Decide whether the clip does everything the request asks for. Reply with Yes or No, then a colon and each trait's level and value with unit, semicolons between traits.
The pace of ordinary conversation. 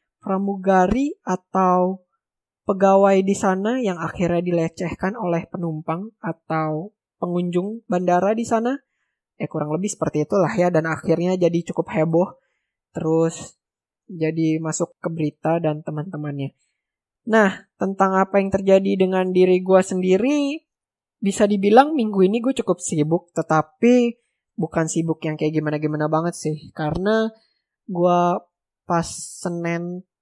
Yes: average, 125 wpm